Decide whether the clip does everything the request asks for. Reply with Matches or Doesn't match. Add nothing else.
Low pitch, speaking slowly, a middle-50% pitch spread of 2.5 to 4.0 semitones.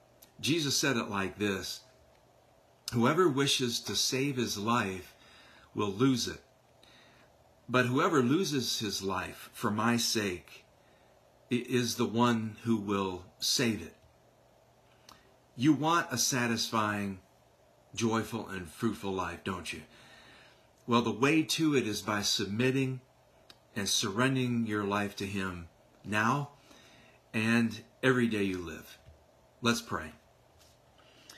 Matches